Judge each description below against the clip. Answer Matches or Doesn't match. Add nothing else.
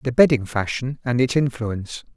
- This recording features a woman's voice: Doesn't match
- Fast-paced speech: Doesn't match